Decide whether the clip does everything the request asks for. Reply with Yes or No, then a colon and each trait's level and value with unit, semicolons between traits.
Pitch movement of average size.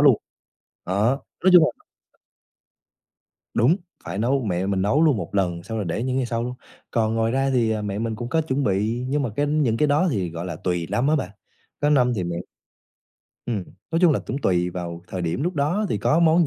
No: wide, 6.8 semitones